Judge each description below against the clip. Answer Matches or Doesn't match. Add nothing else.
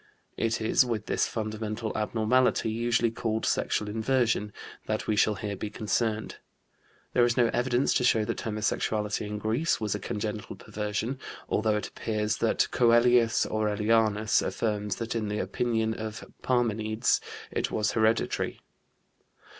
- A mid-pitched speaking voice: Doesn't match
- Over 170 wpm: Doesn't match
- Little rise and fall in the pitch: Matches